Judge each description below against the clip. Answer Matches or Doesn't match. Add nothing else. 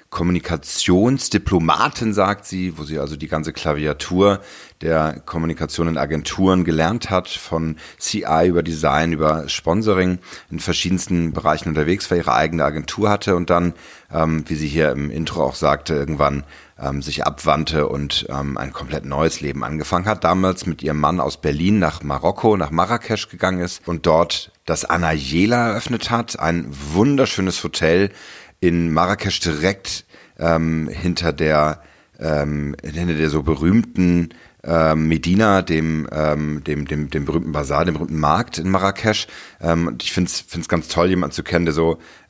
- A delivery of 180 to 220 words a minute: Doesn't match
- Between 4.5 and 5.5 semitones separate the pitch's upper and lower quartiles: Doesn't match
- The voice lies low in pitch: Matches